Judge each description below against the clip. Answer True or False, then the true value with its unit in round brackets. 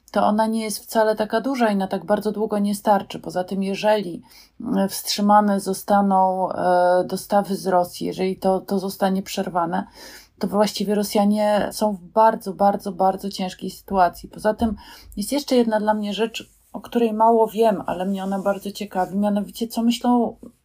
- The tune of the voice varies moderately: False (2.3 semitones)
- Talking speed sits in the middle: False (165 wpm)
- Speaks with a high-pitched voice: True (205 Hz)